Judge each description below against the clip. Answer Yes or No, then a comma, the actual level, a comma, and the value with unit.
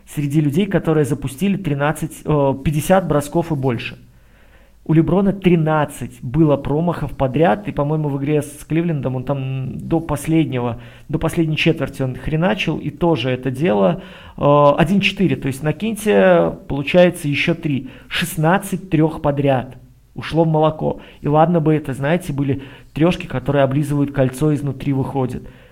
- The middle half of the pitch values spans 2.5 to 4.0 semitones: Yes, average, 3.4 semitones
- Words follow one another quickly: No, average, 140 wpm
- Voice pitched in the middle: Yes, medium, 150 Hz